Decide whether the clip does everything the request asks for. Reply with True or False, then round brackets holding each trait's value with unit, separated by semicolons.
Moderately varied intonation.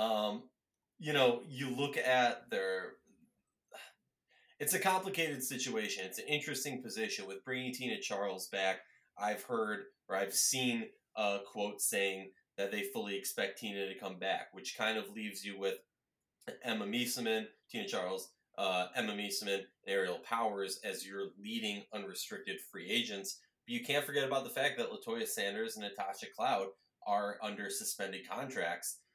False (6.6 semitones)